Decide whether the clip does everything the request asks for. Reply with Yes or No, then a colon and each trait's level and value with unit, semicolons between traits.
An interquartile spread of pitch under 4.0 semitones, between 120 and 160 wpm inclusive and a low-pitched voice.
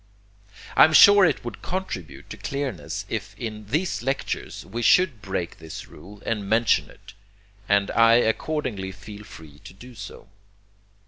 No: average, 5.1 semitones; average, 150 wpm; low, 110 Hz